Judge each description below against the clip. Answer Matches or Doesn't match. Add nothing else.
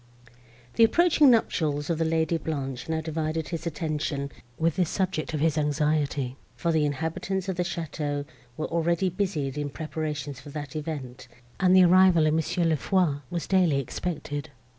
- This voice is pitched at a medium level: Matches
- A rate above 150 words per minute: Matches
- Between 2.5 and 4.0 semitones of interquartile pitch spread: Matches